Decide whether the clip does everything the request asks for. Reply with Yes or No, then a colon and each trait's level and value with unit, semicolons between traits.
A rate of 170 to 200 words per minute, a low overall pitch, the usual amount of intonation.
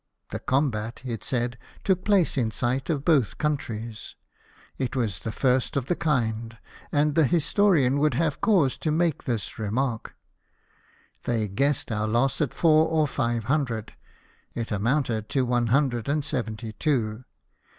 No: average, 160 wpm; low, 130 Hz; average, 4.8 semitones